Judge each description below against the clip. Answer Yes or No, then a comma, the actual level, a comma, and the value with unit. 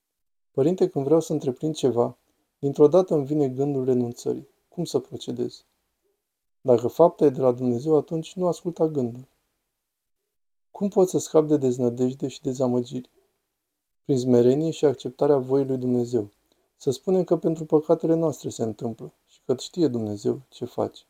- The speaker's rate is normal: Yes, average, 155 wpm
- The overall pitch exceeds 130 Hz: Yes, medium, 140 Hz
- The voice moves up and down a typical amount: Yes, average, 4.6 semitones